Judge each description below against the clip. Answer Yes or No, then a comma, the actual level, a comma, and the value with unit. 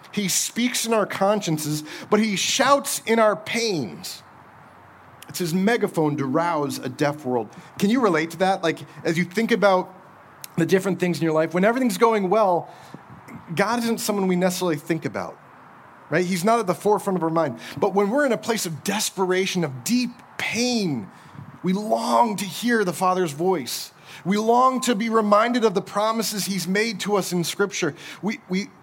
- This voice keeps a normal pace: Yes, average, 185 wpm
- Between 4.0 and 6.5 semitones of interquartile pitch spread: Yes, average, 4.3 semitones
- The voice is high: Yes, high, 195 Hz